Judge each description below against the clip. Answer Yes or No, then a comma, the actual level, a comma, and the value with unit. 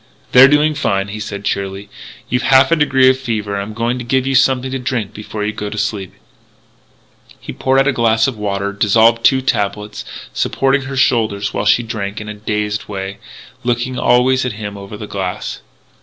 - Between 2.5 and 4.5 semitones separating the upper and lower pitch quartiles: Yes, average, 4.1 semitones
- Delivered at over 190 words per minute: Yes, average, 200 wpm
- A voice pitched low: Yes, low, 110 Hz